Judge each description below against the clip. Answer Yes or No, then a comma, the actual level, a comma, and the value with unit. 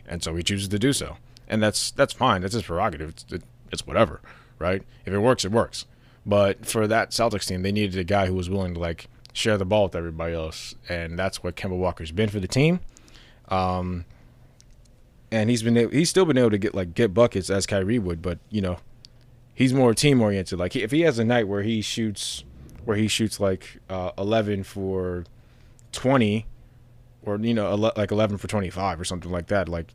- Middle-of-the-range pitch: No, low, 105 Hz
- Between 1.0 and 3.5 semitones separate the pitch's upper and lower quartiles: No, average, 4.4 semitones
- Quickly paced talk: Yes, fast, 215 wpm